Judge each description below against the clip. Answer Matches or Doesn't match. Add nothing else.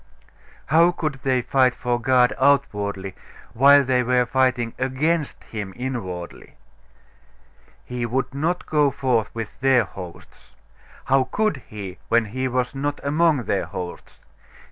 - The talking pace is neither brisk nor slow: Doesn't match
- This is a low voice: Matches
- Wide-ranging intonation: Doesn't match